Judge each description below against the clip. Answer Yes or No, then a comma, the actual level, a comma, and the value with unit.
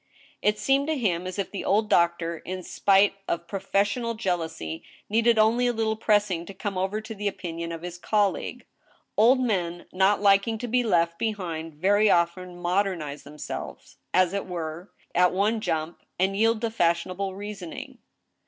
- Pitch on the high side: Yes, high, 195 Hz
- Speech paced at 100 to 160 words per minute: No, average, 170 wpm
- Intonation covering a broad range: No, average, 3.7 semitones